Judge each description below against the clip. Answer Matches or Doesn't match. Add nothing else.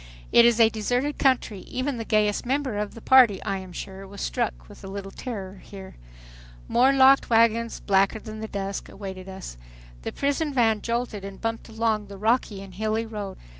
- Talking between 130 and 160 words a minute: Doesn't match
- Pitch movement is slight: Doesn't match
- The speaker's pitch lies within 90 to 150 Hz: Doesn't match